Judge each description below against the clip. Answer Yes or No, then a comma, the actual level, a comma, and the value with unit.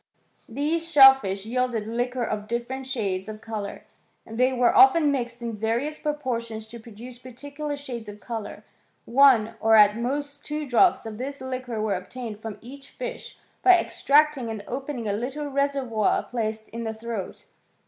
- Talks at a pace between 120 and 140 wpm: No, average, 160 wpm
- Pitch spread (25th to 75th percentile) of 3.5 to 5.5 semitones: Yes, average, 4.0 semitones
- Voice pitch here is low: No, high, 240 Hz